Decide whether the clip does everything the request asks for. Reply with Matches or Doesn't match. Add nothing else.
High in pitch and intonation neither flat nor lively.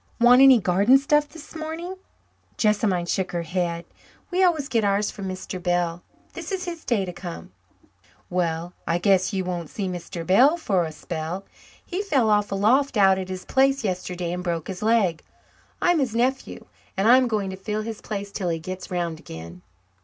Doesn't match